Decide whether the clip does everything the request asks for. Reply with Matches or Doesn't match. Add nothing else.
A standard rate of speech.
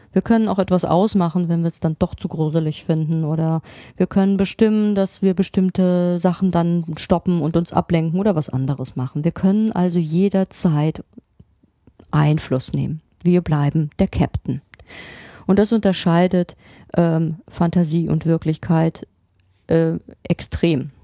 Matches